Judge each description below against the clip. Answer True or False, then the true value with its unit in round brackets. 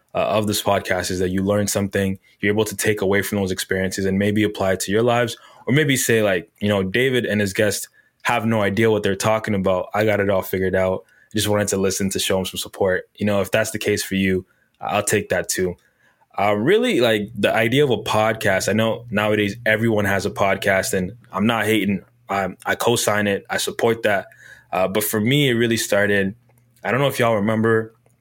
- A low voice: True (105 Hz)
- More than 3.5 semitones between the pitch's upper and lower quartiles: False (2.5 semitones)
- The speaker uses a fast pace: True (230 wpm)